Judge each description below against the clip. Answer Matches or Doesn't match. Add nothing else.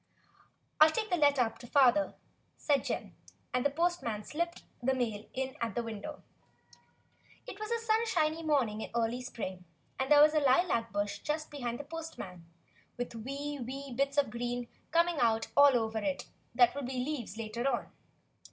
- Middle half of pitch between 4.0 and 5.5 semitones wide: Matches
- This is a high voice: Matches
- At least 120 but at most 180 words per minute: Matches